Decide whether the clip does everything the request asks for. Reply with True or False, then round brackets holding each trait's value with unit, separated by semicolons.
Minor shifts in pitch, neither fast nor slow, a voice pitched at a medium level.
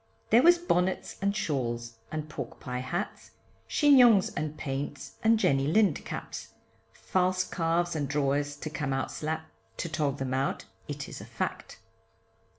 False (5.2 semitones; 155 wpm; 155 Hz)